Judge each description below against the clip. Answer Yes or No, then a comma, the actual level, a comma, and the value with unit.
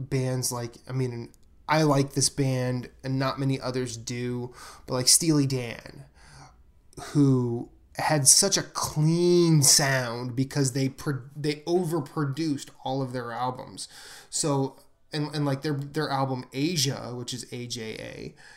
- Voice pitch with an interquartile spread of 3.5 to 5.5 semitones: No, average, 2.8 semitones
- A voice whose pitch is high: No, low, 135 Hz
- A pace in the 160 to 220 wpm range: No, average, 140 wpm